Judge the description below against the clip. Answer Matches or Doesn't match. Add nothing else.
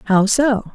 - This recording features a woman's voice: Matches